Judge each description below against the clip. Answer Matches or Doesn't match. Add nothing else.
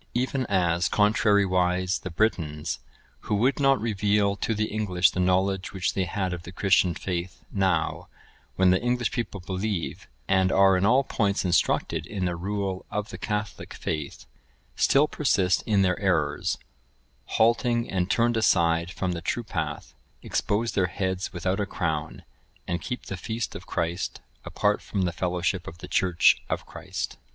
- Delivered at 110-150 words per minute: Doesn't match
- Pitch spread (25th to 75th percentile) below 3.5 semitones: Matches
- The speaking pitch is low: Matches